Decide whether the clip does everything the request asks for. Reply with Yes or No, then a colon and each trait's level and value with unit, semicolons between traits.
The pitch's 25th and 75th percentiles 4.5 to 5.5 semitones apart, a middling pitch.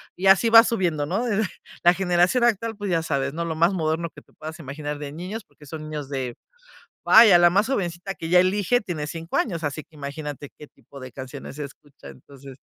Yes: average, 4.8 semitones; medium, 165 Hz